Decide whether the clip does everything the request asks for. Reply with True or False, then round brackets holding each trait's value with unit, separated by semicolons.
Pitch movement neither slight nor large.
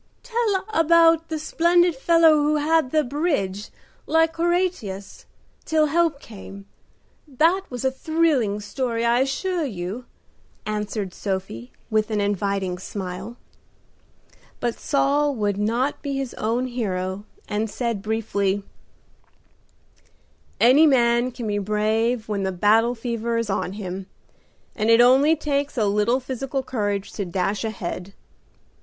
False (6.3 semitones)